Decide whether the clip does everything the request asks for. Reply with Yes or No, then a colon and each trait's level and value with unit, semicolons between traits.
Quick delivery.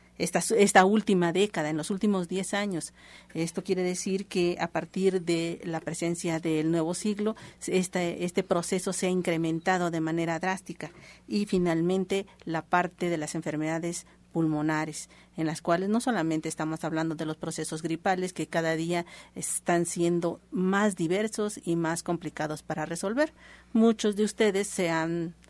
No: average, 155 wpm